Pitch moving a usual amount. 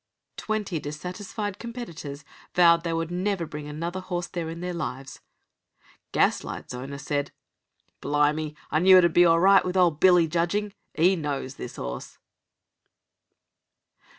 Yes: average, 3.6 semitones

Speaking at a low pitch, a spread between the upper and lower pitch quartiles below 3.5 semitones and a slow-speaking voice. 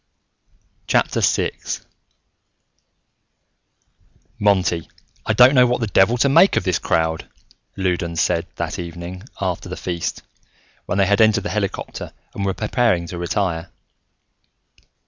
No: very low, 95 Hz; average, 3.8 semitones; slow, 125 wpm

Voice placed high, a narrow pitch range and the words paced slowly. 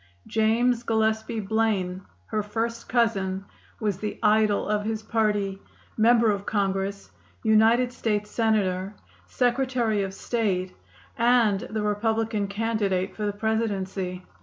Yes: high, 215 Hz; narrow, 2.2 semitones; slow, 115 wpm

